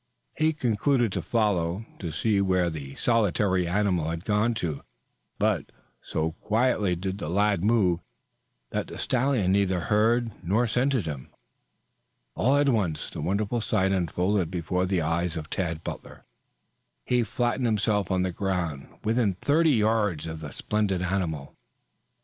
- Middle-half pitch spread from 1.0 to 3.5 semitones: No, average, 4.6 semitones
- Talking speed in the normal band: Yes, average, 145 wpm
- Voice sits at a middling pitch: No, low, 100 Hz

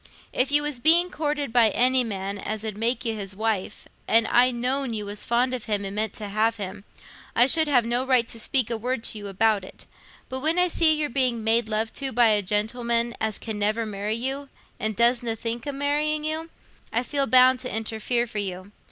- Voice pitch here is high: Yes, high, 235 Hz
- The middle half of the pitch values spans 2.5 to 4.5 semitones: Yes, average, 3.3 semitones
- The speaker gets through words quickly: Yes, fast, 220 wpm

